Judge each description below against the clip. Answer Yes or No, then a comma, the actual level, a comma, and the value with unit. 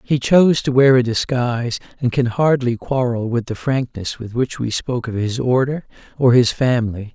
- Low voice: Yes, low, 125 Hz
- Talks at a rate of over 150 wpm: Yes, average, 195 wpm